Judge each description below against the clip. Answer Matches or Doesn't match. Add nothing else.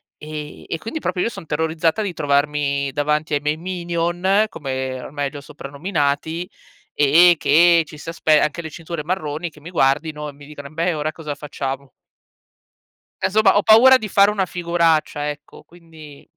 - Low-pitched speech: Doesn't match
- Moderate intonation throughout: Matches